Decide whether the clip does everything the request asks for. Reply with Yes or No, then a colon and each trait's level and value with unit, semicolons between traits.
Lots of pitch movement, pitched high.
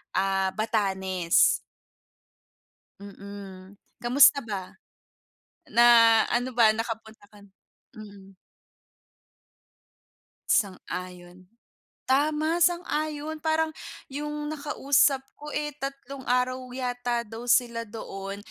Yes: wide, 6.1 semitones; high, 235 Hz